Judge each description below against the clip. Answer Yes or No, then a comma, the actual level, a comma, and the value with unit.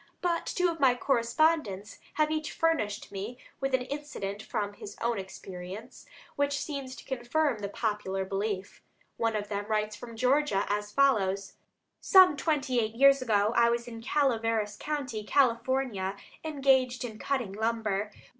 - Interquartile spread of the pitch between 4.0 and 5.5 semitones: Yes, average, 4.9 semitones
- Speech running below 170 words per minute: Yes, average, 150 wpm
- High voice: Yes, high, 235 Hz